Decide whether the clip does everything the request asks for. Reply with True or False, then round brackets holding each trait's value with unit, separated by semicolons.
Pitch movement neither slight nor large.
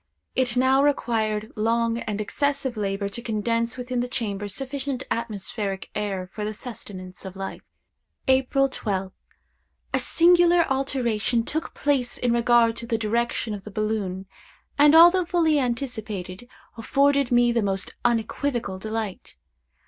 True (3.9 semitones)